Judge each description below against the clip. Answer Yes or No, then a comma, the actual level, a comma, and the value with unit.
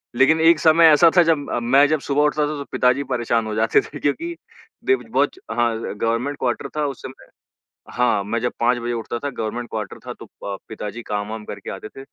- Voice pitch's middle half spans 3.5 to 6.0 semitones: Yes, average, 4.4 semitones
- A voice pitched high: No, low, 125 Hz